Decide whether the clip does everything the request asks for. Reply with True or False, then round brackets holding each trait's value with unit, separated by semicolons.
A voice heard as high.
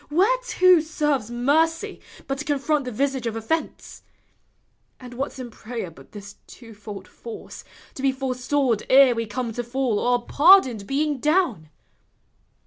True (260 Hz)